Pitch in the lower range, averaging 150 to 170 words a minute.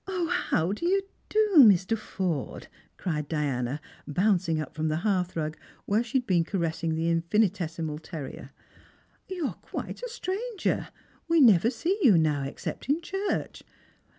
No: medium, 185 Hz; average, 160 wpm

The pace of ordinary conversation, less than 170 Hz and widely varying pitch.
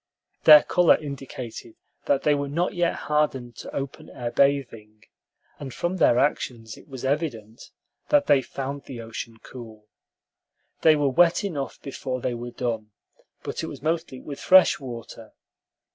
No: average, 155 wpm; low, 135 Hz; average, 4.1 semitones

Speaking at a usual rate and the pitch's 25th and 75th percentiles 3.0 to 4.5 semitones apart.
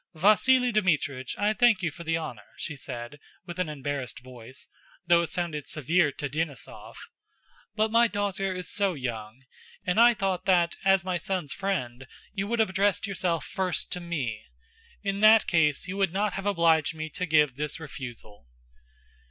No: average, 170 wpm; average, 5.2 semitones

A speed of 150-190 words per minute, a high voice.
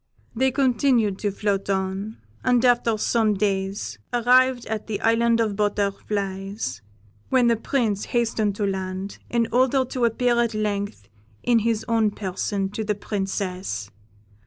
No: average, 140 wpm; high, 215 Hz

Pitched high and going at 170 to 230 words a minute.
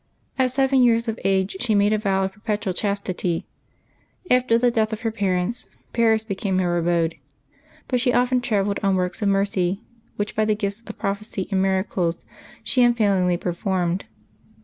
Yes: high, 200 Hz; average, 175 wpm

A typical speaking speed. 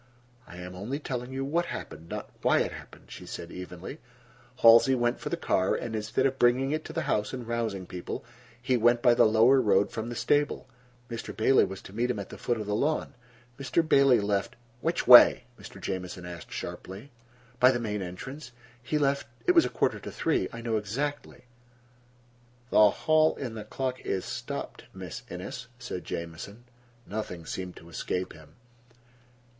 Yes: average, 180 wpm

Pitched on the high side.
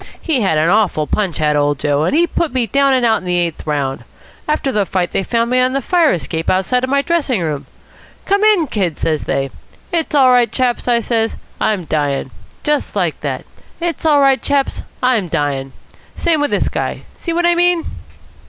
Yes: high, 235 Hz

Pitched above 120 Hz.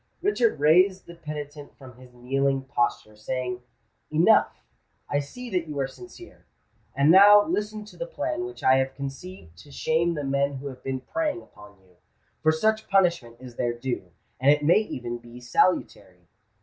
Yes: medium, 140 Hz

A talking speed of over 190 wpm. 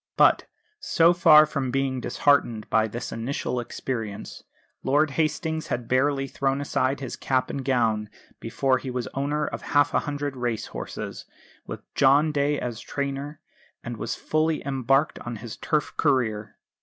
No: average, 155 wpm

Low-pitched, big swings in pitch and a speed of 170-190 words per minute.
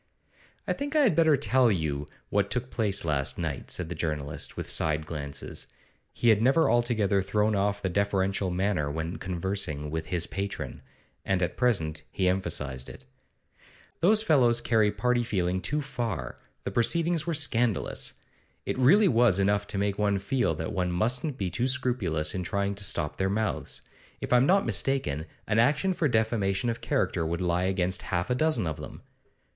Yes: low, 100 Hz; wide, 5.8 semitones; average, 175 wpm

